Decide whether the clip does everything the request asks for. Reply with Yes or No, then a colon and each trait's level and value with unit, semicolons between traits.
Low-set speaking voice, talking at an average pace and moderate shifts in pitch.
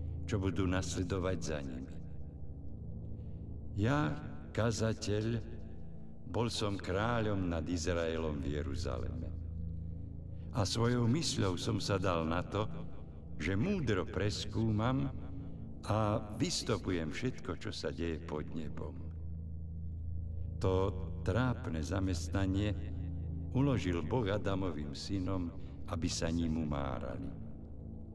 No: very low, 85 Hz; slow, 95 wpm; average, 3.9 semitones